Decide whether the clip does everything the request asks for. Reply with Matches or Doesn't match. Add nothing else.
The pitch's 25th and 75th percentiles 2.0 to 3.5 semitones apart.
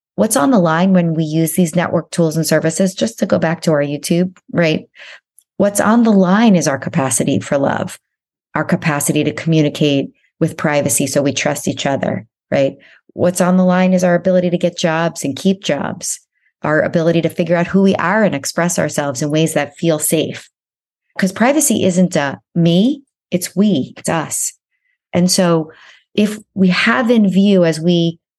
Matches